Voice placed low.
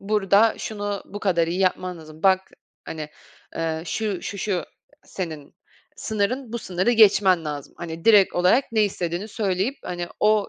No: high, 190 Hz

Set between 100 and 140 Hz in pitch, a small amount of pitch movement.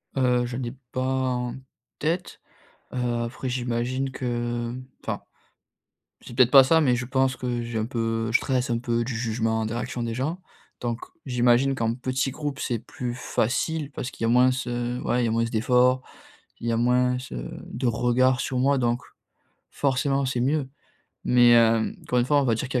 Yes: low, 125 Hz; narrow, 1.8 semitones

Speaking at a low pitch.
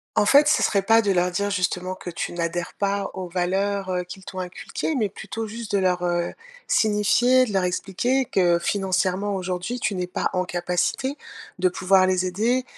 No: high, 190 Hz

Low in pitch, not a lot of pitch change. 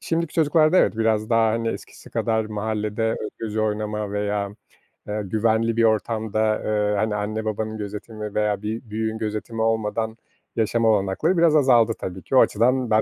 Yes: low, 110 Hz; narrow, 1.3 semitones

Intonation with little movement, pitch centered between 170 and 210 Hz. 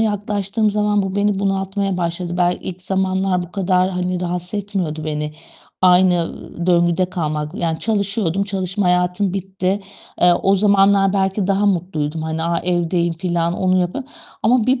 Yes: narrow, 2.3 semitones; medium, 185 Hz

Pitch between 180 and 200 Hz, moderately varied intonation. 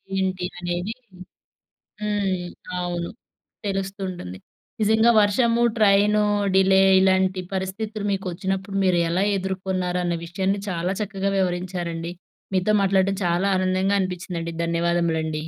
No: high, 190 Hz; narrow, 2.0 semitones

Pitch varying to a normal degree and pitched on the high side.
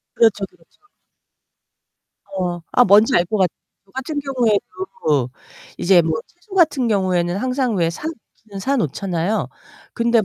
No: wide, 6.5 semitones; high, 210 Hz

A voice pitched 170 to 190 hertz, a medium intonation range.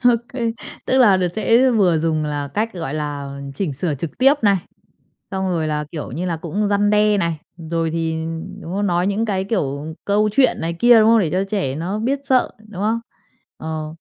Yes: medium, 185 Hz; average, 5.0 semitones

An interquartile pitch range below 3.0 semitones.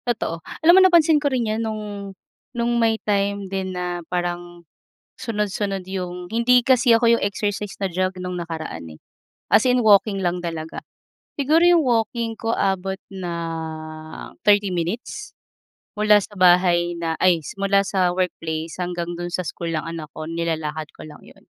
No: average, 4.2 semitones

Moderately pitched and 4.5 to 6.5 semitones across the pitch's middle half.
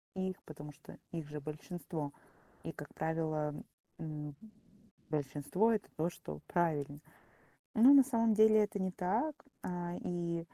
Yes: medium, 170 Hz; average, 4.9 semitones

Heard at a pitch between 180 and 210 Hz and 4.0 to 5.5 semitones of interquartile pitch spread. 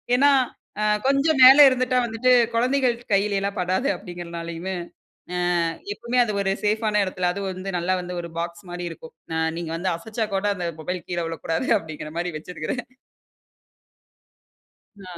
Yes: high, 190 Hz; average, 5.0 semitones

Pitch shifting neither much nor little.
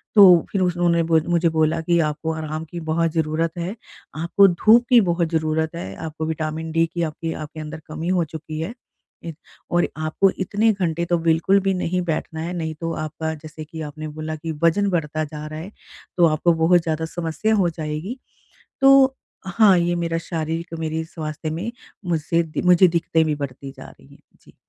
No: narrow, 1.9 semitones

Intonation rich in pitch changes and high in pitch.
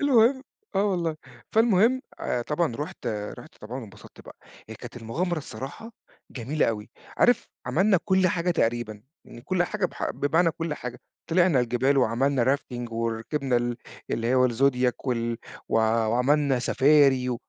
No: wide, 6.2 semitones; low, 135 Hz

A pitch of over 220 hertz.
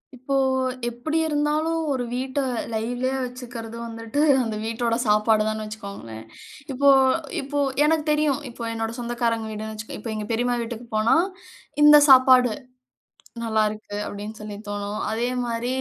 Yes: high, 235 Hz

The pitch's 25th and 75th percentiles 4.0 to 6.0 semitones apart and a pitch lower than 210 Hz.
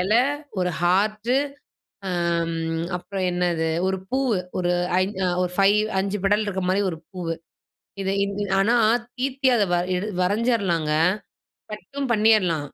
No: average, 3.2 semitones; high, 195 Hz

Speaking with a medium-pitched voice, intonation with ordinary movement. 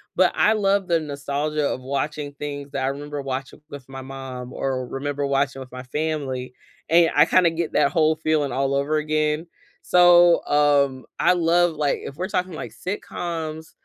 Yes: medium, 145 Hz; average, 3.0 semitones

